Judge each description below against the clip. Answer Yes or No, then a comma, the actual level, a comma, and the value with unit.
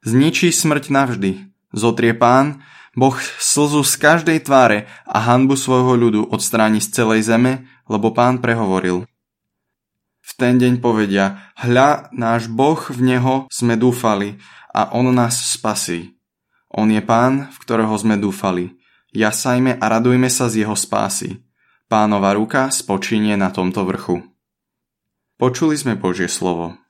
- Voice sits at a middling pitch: No, low, 115 Hz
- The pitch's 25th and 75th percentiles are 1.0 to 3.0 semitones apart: No, average, 3.4 semitones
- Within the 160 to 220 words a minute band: No, average, 135 wpm